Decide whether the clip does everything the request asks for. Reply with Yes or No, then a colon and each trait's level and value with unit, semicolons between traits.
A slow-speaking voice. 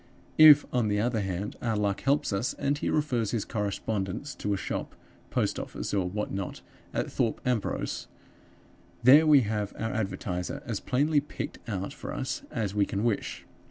No: average, 175 wpm